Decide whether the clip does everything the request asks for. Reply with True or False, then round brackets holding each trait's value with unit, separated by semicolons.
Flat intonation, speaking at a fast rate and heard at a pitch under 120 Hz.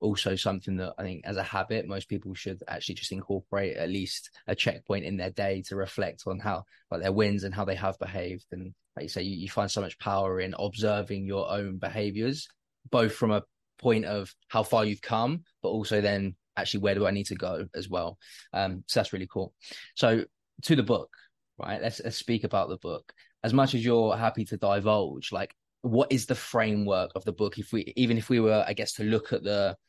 True (2.3 semitones; 225 wpm; 100 Hz)